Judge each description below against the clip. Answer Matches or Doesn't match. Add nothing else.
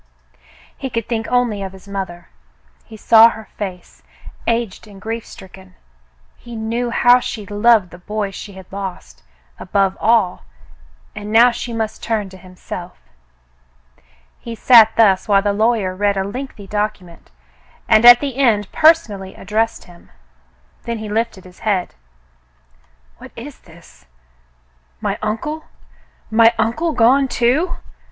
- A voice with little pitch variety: Doesn't match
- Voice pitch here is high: Matches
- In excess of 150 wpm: Doesn't match